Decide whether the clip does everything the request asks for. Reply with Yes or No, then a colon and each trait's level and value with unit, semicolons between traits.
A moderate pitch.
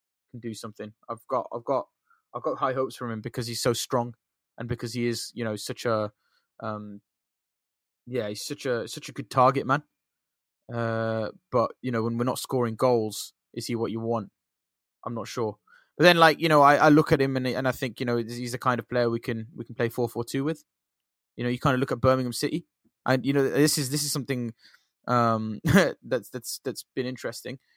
No: low, 120 Hz